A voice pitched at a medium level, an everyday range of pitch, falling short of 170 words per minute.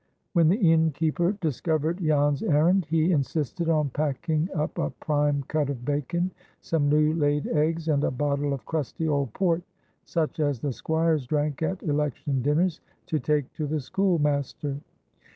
No: medium, 150 Hz; narrow, 2.2 semitones; average, 155 wpm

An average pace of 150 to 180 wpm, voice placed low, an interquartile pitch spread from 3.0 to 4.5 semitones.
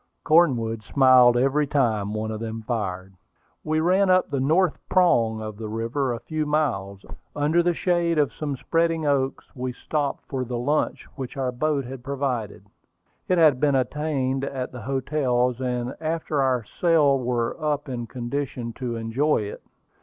Yes: average, 165 wpm; low, 130 Hz; average, 4.2 semitones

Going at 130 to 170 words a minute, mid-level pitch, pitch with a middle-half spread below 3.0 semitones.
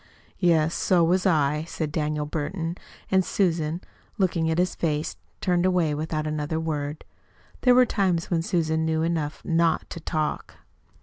Yes: average, 150 wpm; medium, 160 Hz; narrow, 2.4 semitones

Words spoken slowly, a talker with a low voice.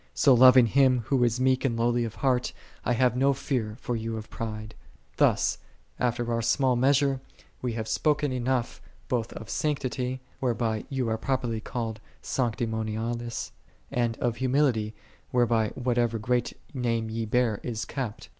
No: average, 165 wpm; low, 120 Hz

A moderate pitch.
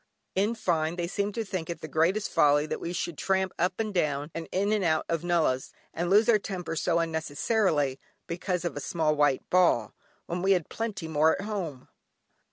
Yes: medium, 170 Hz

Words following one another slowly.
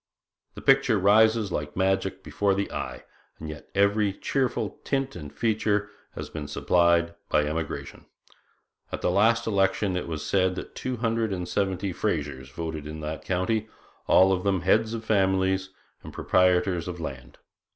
No: average, 160 wpm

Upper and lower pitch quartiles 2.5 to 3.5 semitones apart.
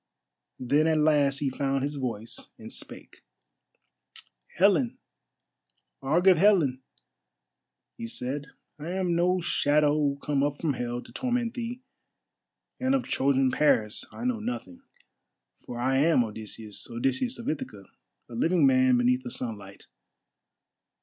No: wide, 5.6 semitones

